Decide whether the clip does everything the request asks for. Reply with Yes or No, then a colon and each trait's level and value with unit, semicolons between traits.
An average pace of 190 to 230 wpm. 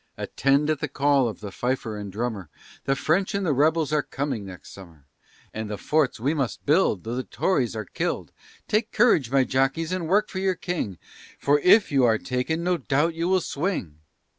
Yes: average, 200 wpm